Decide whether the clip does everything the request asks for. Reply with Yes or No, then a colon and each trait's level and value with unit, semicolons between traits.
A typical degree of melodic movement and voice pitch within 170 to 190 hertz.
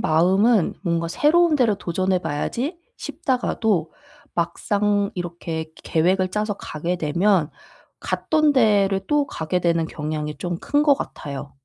Yes: average, 4.7 semitones; medium, 185 Hz